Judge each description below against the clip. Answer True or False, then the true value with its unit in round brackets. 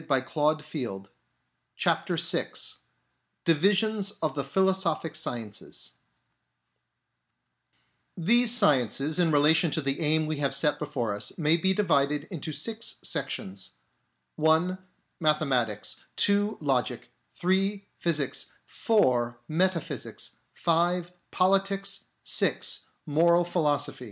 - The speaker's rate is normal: False (100 wpm)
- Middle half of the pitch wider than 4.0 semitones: True (4.7 semitones)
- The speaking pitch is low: False (155 Hz)